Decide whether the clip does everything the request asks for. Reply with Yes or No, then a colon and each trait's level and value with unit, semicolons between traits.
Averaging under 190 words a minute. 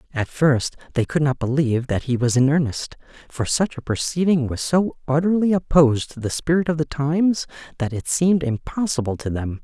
No: average, 195 wpm